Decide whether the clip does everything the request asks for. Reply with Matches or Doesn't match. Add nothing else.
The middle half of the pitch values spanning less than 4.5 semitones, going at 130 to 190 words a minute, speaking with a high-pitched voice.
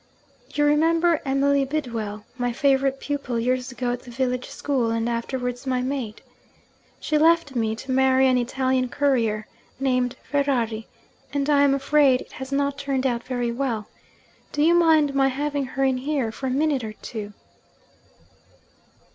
Matches